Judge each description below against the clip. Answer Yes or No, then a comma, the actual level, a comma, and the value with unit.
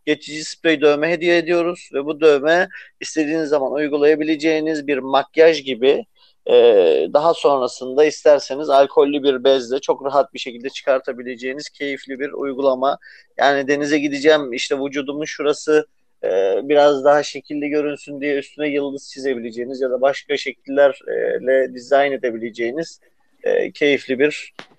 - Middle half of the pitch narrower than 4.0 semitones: Yes, narrow, 2.5 semitones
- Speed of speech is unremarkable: Yes, average, 120 wpm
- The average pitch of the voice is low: No, medium, 145 Hz